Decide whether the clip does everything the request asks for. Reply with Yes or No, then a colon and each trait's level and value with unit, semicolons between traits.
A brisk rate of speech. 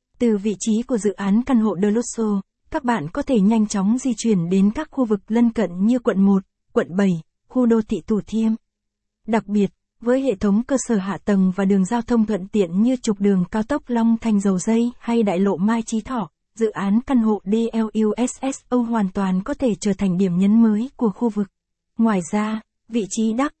No: average, 220 wpm